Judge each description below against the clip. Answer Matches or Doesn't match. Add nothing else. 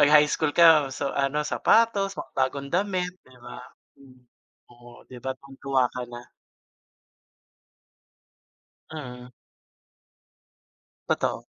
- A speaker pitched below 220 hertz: Matches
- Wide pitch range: Doesn't match